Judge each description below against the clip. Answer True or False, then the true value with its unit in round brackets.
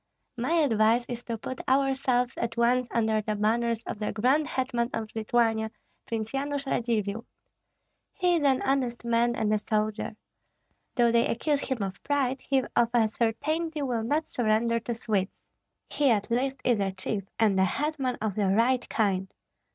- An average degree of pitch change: True (3.3 semitones)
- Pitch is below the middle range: False (235 Hz)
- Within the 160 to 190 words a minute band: True (170 wpm)